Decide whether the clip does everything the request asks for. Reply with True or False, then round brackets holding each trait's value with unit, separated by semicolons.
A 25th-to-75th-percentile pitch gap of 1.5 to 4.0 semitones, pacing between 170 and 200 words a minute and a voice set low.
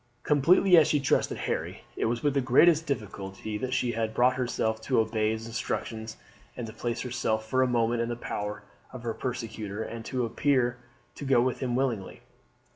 True (2.8 semitones; 190 wpm; 120 Hz)